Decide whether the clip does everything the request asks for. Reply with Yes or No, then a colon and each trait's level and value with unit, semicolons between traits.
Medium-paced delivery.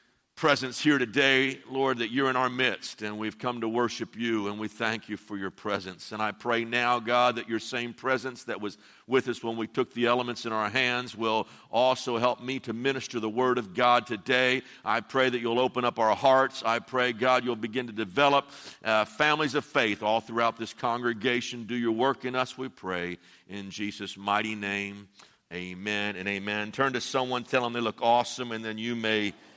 No: fast, 210 wpm